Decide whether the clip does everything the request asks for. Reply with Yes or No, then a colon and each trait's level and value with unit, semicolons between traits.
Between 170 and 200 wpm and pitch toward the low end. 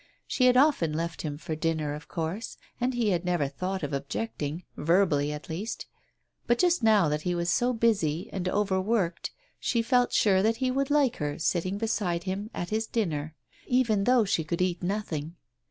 No: average, 190 wpm; medium, 185 Hz